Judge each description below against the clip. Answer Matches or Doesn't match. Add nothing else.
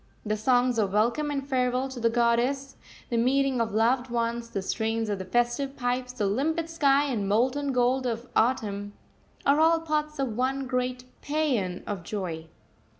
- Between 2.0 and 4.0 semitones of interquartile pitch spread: Matches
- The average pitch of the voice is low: Doesn't match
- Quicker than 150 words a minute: Matches